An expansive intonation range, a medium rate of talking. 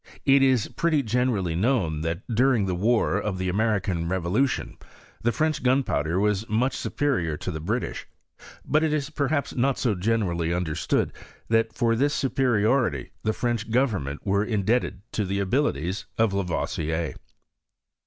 Yes: wide, 5.7 semitones; average, 155 wpm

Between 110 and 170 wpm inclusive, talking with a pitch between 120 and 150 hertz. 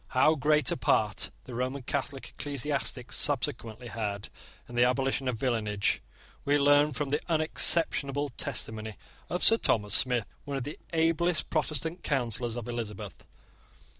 Yes: average, 140 wpm; low, 135 Hz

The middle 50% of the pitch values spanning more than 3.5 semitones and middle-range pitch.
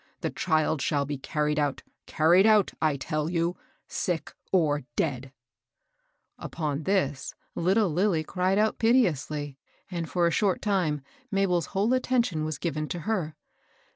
Yes: average, 4.2 semitones; medium, 165 Hz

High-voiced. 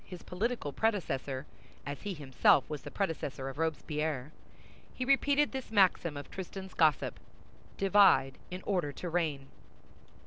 No: medium, 165 Hz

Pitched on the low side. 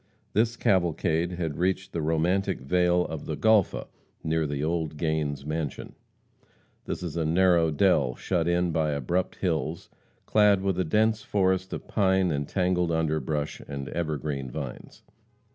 Yes: very low, 85 Hz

